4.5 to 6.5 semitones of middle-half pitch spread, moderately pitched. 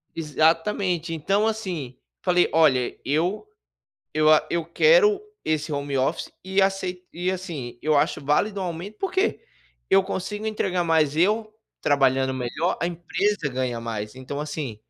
Yes: average, 5.1 semitones; medium, 165 Hz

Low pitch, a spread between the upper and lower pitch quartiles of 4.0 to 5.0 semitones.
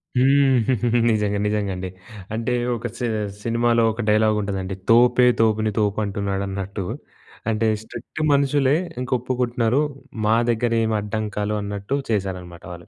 No: low, 110 Hz; average, 3.2 semitones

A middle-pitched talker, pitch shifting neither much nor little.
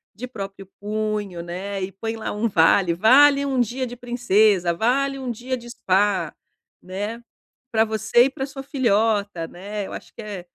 No: high, 215 Hz; average, 3.8 semitones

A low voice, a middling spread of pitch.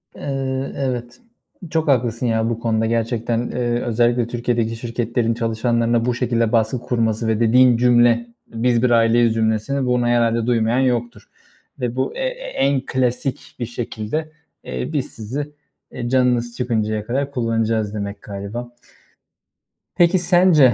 No: low, 120 Hz; narrow, 1.7 semitones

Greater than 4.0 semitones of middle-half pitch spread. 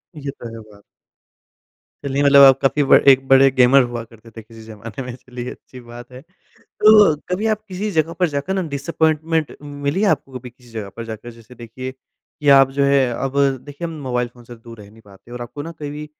No: average, 3.4 semitones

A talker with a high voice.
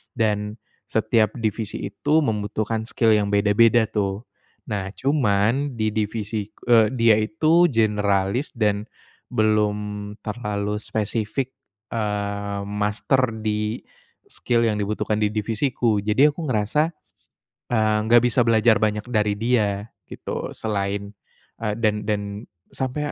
No: low, 110 Hz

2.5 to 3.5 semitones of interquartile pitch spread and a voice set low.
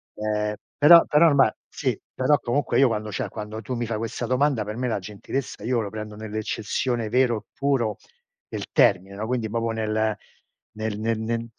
Yes: average, 2.8 semitones; low, 110 Hz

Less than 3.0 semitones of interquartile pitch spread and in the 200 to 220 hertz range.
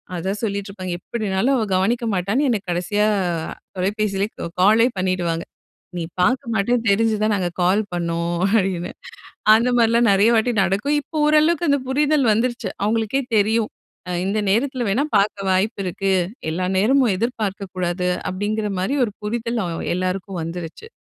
No: average, 4.0 semitones; high, 210 Hz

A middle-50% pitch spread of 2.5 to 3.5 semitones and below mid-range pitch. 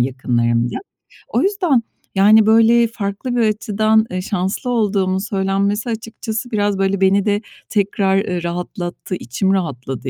No: average, 3.1 semitones; high, 200 Hz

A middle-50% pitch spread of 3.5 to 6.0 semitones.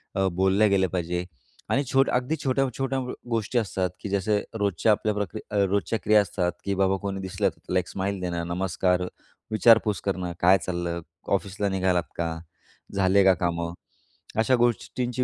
No: average, 2.9 semitones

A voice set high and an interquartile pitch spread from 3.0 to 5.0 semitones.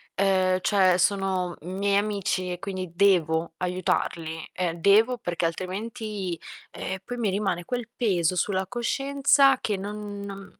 No: high, 195 Hz; narrow, 2.6 semitones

